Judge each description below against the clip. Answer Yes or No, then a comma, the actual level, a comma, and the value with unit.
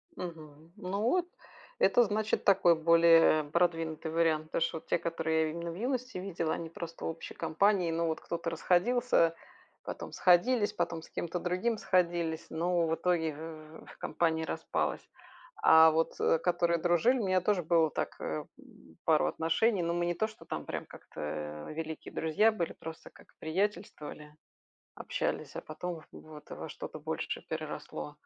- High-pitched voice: No, medium, 170 Hz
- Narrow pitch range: Yes, narrow, 2.3 semitones